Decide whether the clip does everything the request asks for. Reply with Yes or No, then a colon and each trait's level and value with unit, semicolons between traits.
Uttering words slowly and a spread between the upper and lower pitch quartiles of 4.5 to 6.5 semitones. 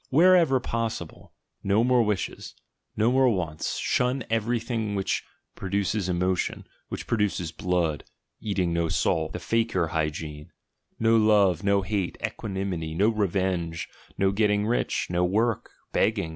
No: slow, 130 wpm; average, 4.1 semitones